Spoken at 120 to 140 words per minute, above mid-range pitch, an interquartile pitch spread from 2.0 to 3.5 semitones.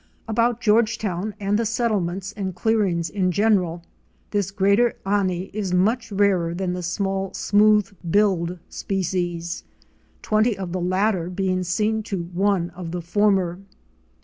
Yes: slow, 135 wpm; high, 195 Hz; average, 2.8 semitones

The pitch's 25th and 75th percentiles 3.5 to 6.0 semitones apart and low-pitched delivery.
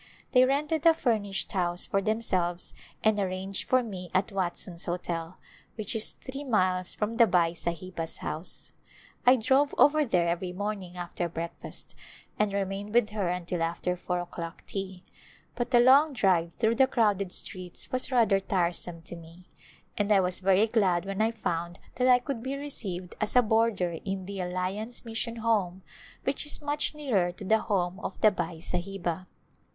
No: average, 4.4 semitones; high, 195 Hz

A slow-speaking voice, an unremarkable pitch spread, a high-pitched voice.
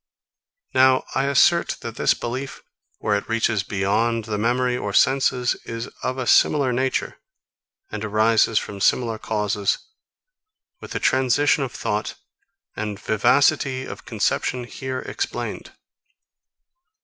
No: slow, 125 wpm; average, 3.3 semitones; low, 120 Hz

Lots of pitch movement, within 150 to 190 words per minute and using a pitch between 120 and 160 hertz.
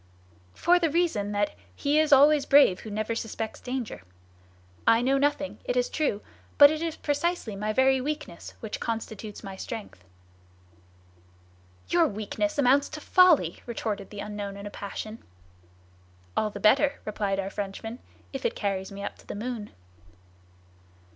No: wide, 6.0 semitones; average, 155 wpm; high, 230 Hz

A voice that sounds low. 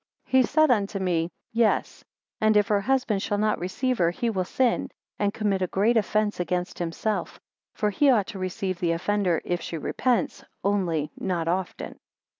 No: high, 200 Hz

